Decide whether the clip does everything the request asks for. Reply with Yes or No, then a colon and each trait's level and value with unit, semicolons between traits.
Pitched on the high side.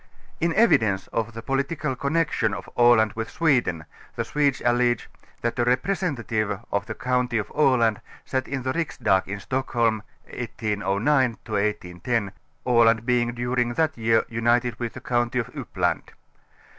No: low, 120 Hz